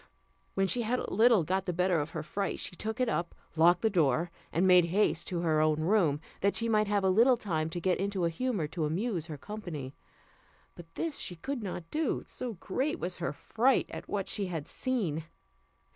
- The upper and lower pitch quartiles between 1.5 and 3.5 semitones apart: No, average, 4.8 semitones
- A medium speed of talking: No, fast, 220 wpm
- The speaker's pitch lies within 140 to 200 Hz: Yes, medium, 185 Hz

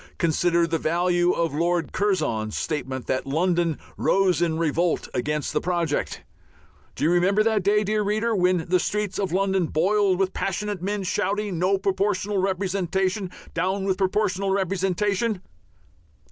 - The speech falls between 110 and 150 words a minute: Yes, average, 145 wpm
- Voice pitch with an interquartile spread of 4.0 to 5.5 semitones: No, average, 2.7 semitones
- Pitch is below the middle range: No, medium, 185 Hz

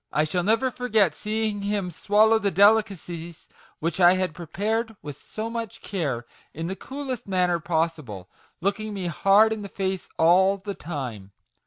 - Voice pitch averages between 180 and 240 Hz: Yes, high, 190 Hz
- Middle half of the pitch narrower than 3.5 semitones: No, average, 4.4 semitones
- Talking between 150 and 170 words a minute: Yes, average, 165 wpm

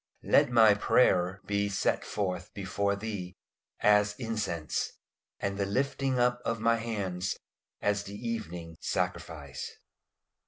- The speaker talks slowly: Yes, slow, 120 wpm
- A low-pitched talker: Yes, low, 100 Hz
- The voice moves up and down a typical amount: Yes, average, 3.8 semitones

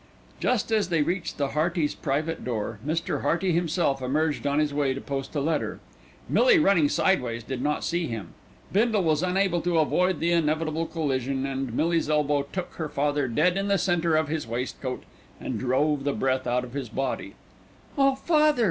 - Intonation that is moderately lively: Yes, average, 4.3 semitones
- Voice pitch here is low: No, medium, 155 Hz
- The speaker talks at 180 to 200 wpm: Yes, average, 185 wpm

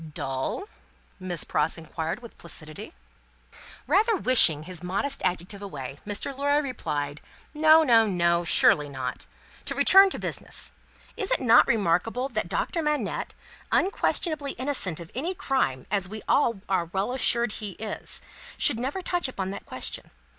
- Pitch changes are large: Yes, wide, 8.5 semitones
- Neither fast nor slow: Yes, average, 145 wpm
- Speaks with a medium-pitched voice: No, high, 210 Hz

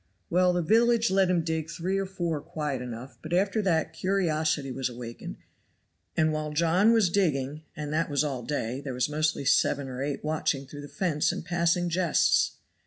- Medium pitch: Yes, medium, 155 Hz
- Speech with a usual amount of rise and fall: Yes, average, 4.0 semitones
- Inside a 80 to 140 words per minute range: No, average, 185 wpm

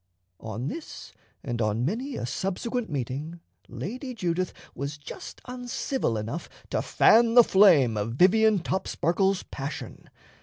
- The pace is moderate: No, slow, 125 wpm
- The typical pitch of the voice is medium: Yes, medium, 180 Hz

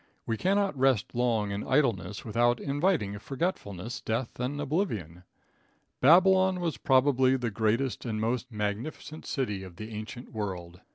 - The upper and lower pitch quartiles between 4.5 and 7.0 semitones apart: Yes, average, 5.3 semitones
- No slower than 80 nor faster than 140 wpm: Yes, slow, 135 wpm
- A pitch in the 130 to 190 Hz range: No, low, 120 Hz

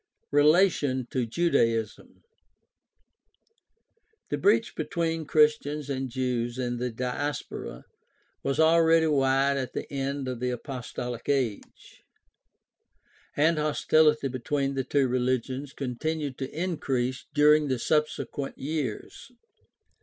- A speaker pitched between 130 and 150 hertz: Yes, medium, 140 Hz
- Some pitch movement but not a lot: Yes, average, 3.2 semitones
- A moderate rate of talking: No, slow, 110 wpm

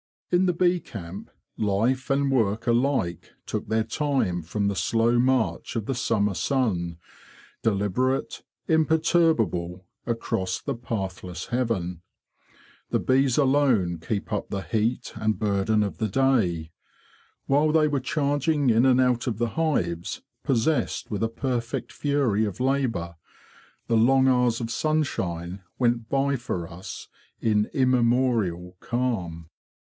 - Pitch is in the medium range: No, low, 115 Hz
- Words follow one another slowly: Yes, slow, 130 wpm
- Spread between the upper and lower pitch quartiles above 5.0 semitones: Yes, wide, 5.4 semitones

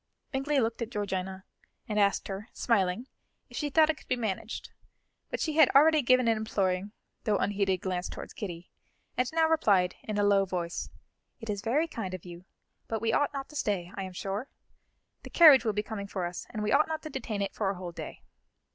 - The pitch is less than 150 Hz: No, high, 210 Hz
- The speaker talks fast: Yes, fast, 215 wpm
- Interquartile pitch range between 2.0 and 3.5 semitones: No, average, 5.1 semitones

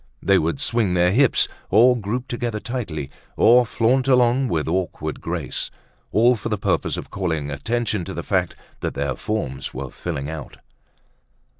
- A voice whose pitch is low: Yes, low, 105 Hz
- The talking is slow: No, average, 160 wpm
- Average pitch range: No, wide, 7.0 semitones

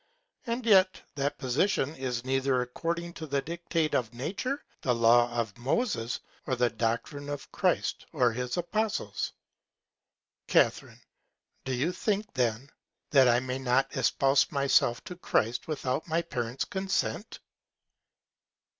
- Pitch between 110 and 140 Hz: Yes, low, 135 Hz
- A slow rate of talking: Yes, slow, 130 wpm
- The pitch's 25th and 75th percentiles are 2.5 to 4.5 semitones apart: No, wide, 5.6 semitones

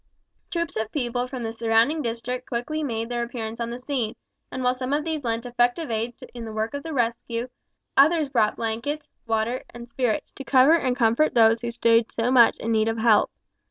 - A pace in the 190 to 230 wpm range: Yes, average, 200 wpm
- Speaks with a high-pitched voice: Yes, high, 240 Hz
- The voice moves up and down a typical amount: No, narrow, 2.3 semitones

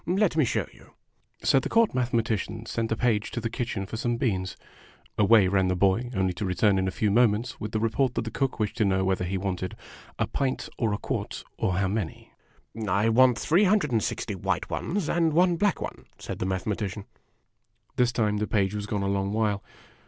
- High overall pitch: No, low, 110 Hz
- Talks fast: Yes, fast, 225 wpm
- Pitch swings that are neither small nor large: Yes, average, 3.9 semitones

